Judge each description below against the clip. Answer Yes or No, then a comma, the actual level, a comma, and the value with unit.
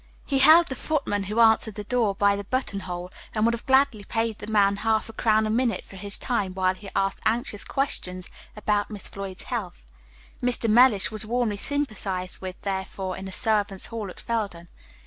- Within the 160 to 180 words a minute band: No, average, 195 wpm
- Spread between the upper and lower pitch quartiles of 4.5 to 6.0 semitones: No, average, 3.2 semitones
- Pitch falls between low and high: No, high, 210 Hz